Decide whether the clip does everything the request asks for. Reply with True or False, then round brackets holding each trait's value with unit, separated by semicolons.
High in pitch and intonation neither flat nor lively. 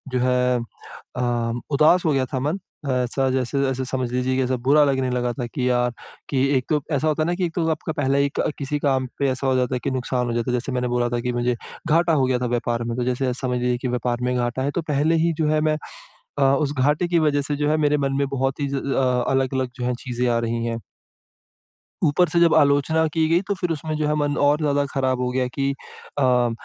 False (135 Hz; 3.0 semitones)